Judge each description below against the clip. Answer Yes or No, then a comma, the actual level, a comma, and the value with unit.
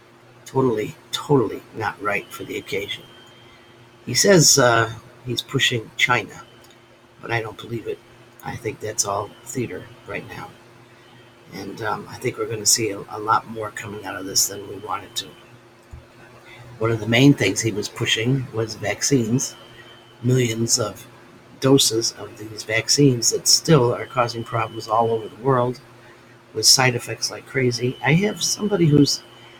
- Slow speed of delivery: No, average, 160 wpm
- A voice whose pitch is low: Yes, low, 120 Hz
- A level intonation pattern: Yes, narrow, 1.6 semitones